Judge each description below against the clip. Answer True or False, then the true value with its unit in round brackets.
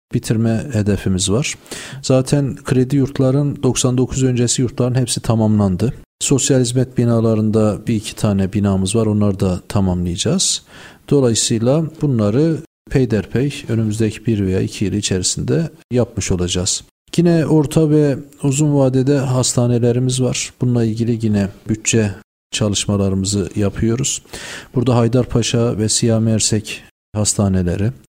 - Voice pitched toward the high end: False (115 Hz)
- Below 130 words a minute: True (110 wpm)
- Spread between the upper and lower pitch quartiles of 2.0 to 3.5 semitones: False (4.1 semitones)